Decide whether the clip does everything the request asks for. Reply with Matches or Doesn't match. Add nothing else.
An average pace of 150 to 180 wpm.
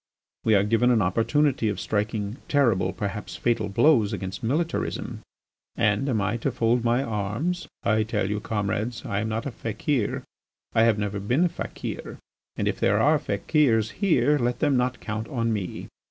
Matches